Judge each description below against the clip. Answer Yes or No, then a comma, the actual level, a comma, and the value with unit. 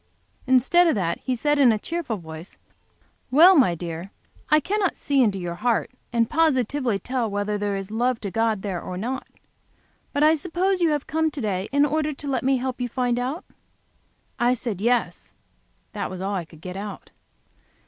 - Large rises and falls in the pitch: Yes, wide, 6.4 semitones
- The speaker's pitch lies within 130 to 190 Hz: No, high, 245 Hz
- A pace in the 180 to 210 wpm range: Yes, average, 200 wpm